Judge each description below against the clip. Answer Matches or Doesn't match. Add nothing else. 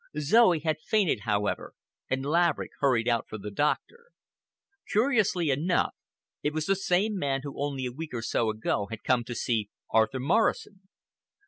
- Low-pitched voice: Doesn't match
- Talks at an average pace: Matches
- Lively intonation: Matches